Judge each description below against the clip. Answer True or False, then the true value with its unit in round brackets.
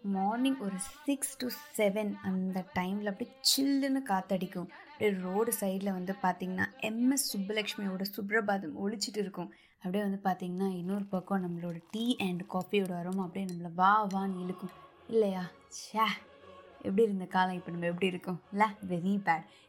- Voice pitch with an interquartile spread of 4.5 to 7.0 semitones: False (2.7 semitones)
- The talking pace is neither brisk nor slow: False (145 wpm)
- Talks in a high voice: True (195 Hz)